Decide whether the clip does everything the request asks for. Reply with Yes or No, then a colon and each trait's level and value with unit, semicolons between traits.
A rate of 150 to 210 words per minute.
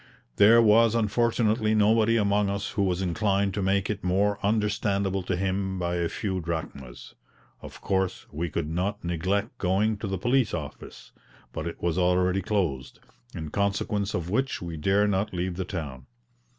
Yes: average, 165 wpm